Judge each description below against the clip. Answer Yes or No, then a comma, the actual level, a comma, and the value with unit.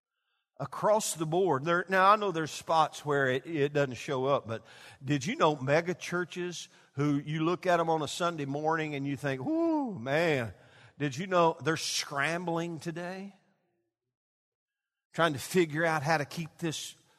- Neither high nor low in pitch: Yes, medium, 160 Hz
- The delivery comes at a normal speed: Yes, average, 170 wpm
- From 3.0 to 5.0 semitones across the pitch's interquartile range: Yes, average, 3.5 semitones